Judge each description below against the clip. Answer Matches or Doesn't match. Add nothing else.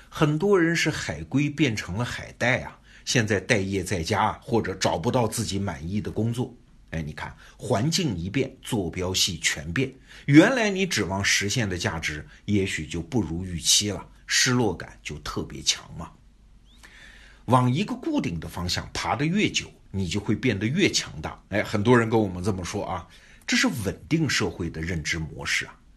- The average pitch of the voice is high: Doesn't match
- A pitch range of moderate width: Doesn't match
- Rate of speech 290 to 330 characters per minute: Doesn't match